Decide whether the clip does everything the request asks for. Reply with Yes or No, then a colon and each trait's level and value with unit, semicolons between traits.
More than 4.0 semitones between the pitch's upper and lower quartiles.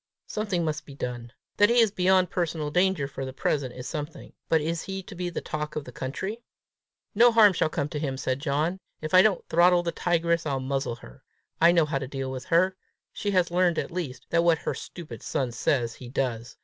Yes: average, 4.9 semitones